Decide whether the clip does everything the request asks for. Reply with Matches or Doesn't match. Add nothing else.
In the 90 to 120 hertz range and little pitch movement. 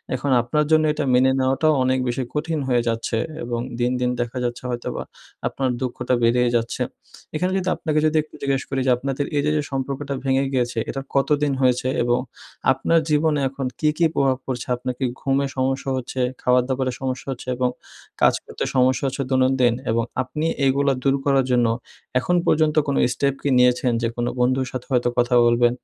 Doesn't match